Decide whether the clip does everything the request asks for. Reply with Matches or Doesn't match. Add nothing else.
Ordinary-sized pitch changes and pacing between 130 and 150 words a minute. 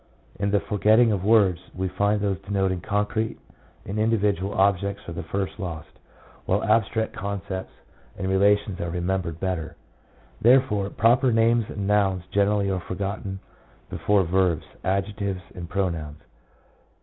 Doesn't match